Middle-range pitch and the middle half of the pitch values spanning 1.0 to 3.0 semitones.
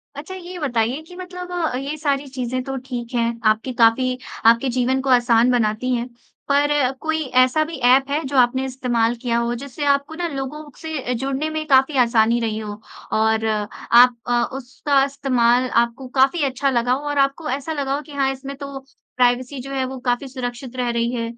No: very high, 260 Hz; average, 2.7 semitones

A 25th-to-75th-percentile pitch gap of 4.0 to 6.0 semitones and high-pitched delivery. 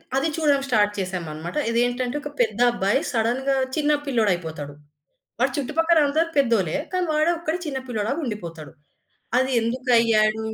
Yes: wide, 5.5 semitones; high, 245 Hz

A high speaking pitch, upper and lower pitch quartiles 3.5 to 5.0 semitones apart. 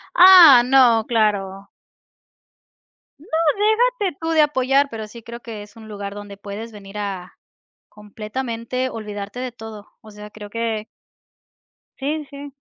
Yes: high, 225 Hz; average, 3.8 semitones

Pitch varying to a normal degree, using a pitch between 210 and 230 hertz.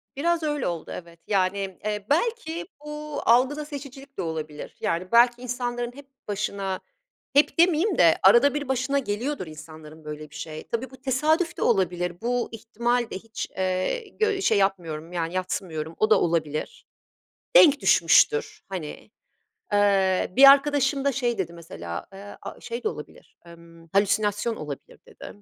No: wide, 8.2 semitones; high, 215 Hz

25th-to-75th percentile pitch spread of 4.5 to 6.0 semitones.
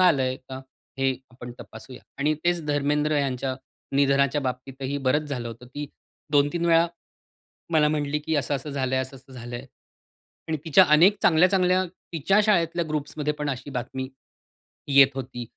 No: average, 3.1 semitones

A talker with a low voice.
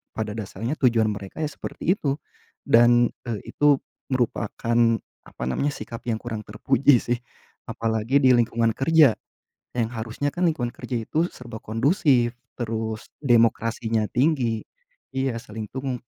Yes: low, 120 Hz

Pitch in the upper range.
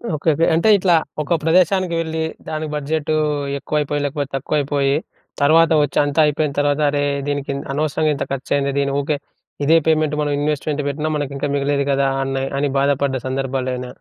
No: medium, 145 Hz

